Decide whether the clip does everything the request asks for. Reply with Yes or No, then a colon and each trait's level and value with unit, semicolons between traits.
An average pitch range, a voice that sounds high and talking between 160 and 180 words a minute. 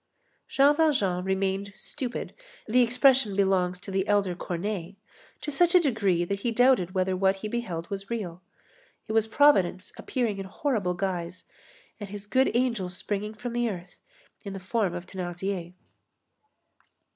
No: average, 4.4 semitones; high, 200 Hz; average, 145 wpm